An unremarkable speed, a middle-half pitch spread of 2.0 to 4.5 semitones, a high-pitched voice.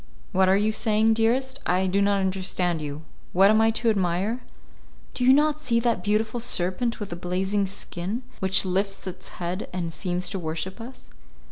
Yes: average, 180 wpm; average, 3.6 semitones; high, 195 Hz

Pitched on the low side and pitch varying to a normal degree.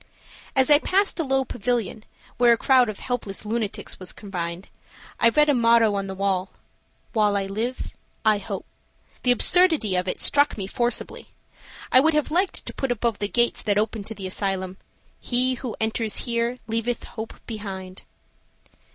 No: high, 225 Hz; average, 3.9 semitones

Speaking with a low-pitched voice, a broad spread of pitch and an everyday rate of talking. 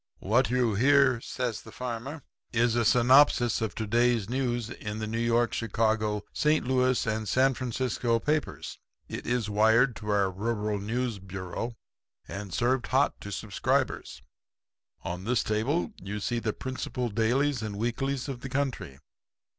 No: low, 115 Hz; average, 3.1 semitones; average, 155 wpm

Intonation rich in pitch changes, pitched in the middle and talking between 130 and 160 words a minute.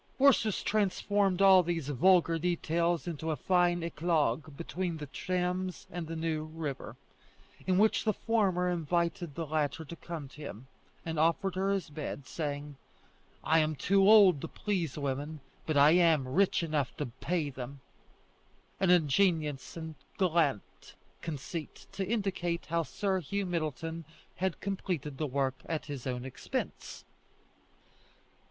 No: average, 3.6 semitones; medium, 165 Hz; average, 145 wpm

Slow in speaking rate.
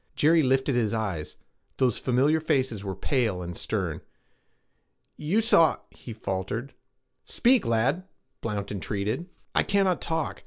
Yes: slow, 125 wpm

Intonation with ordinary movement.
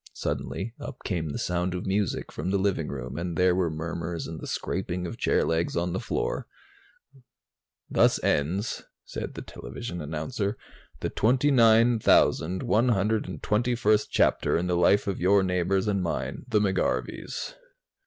Yes: average, 3.7 semitones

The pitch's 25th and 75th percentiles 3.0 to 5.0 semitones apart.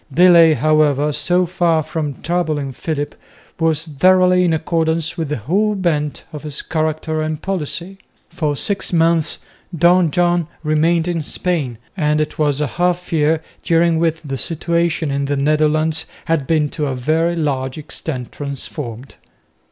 No: narrow, 2.4 semitones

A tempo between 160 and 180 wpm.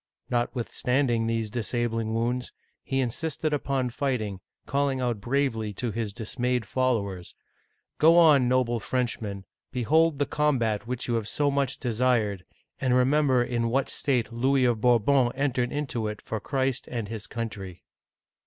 No: average, 145 wpm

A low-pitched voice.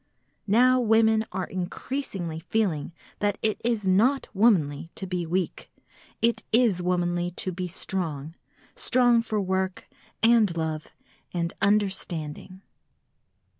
No: high, 190 Hz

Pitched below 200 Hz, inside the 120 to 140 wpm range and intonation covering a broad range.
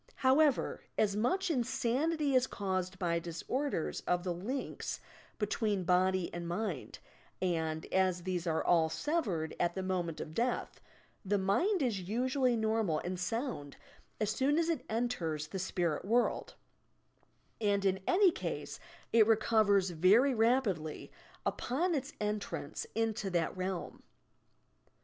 No: high, 205 Hz; slow, 135 wpm; wide, 5.8 semitones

